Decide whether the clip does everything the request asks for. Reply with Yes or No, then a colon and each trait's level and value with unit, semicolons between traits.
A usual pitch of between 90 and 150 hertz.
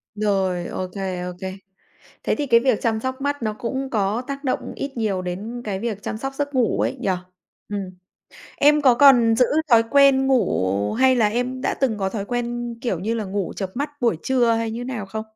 No: high, 230 Hz